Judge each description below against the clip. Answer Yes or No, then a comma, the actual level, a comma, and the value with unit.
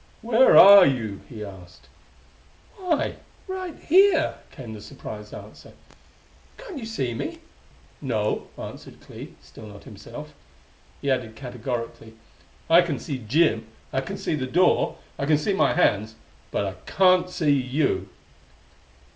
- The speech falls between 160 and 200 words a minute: No, average, 140 wpm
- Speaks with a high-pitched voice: No, low, 135 Hz